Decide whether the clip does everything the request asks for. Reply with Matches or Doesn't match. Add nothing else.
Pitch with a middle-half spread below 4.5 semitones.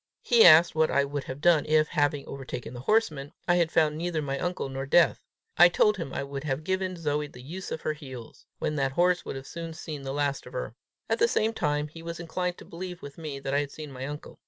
Matches